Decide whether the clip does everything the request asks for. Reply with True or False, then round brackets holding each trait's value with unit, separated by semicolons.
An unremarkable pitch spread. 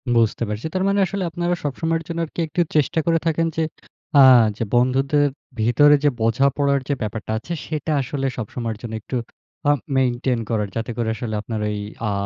False (5.7 semitones)